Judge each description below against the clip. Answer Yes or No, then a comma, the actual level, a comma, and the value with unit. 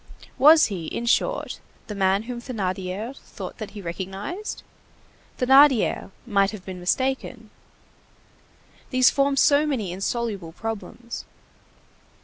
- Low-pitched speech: No, high, 225 Hz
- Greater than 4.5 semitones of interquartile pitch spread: Yes, average, 5.2 semitones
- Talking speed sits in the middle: No, slow, 115 wpm